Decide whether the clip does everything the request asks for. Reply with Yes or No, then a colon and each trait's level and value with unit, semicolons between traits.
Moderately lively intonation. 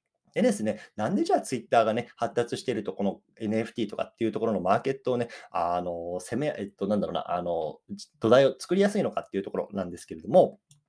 Yes: average, 4.9 semitones